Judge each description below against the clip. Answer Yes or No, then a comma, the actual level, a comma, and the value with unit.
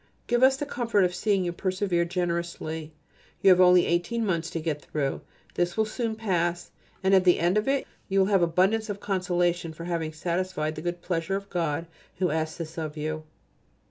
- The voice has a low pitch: No, medium, 175 Hz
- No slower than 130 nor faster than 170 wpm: No, average, 200 wpm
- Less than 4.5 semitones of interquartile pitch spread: Yes, average, 2.8 semitones